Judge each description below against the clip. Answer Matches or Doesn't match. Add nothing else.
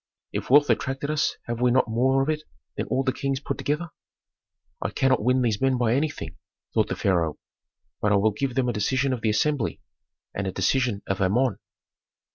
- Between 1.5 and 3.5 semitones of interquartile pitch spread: Doesn't match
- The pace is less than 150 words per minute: Doesn't match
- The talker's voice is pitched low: Matches